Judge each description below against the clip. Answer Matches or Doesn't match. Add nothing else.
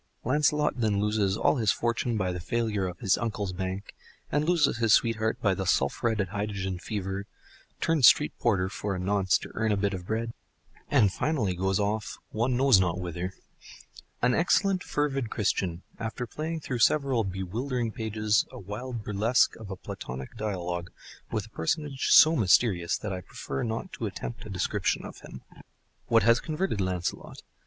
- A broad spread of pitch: Doesn't match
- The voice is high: Doesn't match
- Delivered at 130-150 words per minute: Doesn't match